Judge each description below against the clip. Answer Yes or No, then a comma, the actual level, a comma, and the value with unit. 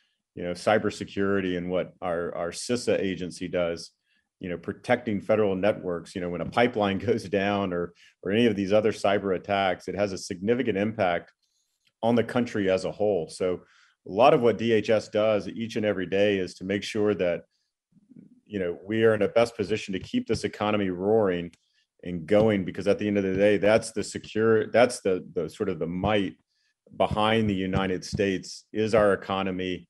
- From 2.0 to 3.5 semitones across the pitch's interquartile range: Yes, average, 2.8 semitones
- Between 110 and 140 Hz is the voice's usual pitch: No, low, 100 Hz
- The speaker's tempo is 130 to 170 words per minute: No, average, 195 wpm